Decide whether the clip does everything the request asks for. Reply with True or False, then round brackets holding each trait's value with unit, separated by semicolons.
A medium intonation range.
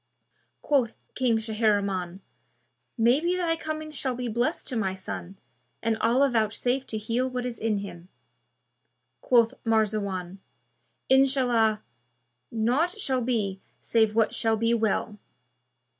True (3.2 semitones)